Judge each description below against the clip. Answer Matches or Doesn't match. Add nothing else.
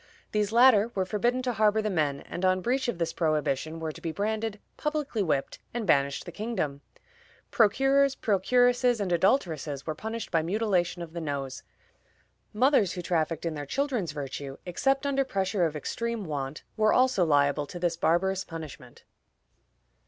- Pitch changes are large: Matches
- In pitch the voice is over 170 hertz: Matches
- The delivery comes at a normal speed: Matches